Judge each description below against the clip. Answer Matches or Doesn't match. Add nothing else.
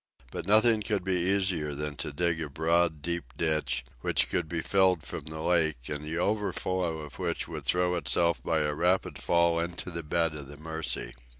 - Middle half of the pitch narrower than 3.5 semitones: Matches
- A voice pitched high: Doesn't match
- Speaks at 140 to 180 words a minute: Doesn't match